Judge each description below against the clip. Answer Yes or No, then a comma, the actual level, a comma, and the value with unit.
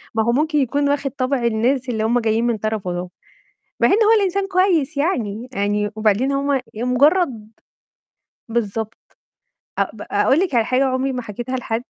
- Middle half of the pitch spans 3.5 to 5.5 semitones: Yes, average, 4.2 semitones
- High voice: Yes, very high, 250 Hz